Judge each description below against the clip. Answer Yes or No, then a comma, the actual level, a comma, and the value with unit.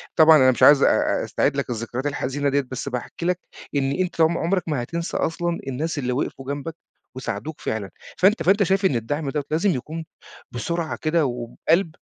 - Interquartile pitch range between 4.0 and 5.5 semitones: Yes, average, 4.5 semitones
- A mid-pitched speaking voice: Yes, medium, 150 Hz